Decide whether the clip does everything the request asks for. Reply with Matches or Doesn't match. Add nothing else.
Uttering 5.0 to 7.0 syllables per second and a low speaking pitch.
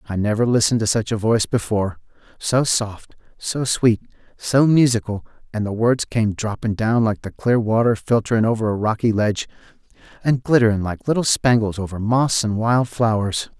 Matches